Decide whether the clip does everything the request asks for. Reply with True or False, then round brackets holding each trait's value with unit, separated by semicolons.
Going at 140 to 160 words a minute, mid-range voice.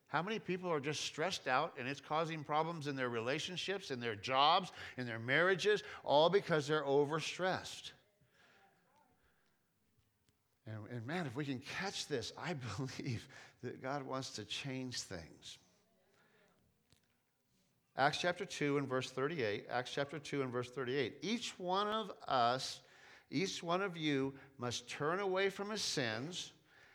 True (145 wpm; 145 Hz)